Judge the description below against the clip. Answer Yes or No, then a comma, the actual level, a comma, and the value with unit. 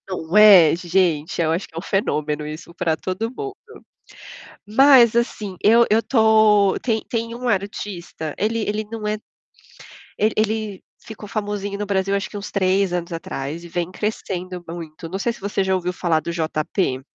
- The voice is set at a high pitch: Yes, high, 195 Hz